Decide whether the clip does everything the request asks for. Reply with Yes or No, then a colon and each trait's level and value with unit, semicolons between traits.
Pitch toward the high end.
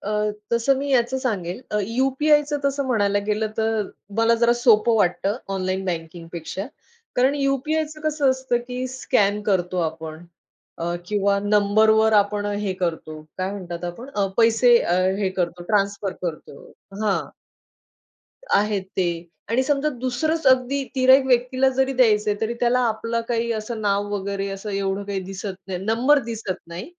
Yes: high, 215 Hz